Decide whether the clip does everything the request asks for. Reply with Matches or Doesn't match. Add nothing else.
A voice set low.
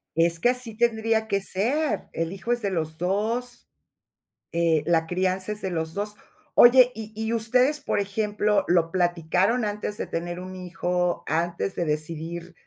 Doesn't match